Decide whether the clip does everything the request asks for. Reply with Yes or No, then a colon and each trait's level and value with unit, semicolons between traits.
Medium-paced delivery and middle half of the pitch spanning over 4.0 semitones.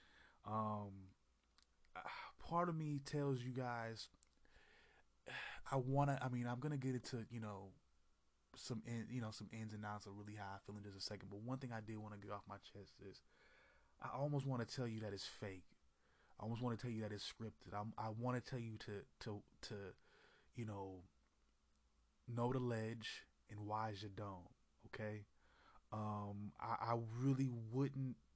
No: average, 185 wpm; average, 3.5 semitones